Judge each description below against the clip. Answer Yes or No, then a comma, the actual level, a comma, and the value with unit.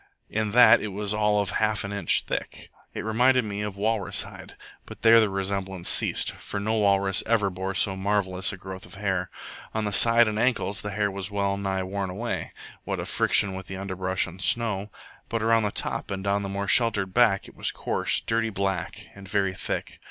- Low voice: Yes, low, 100 Hz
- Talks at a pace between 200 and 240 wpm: Yes, fast, 205 wpm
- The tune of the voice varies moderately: No, narrow, 2.0 semitones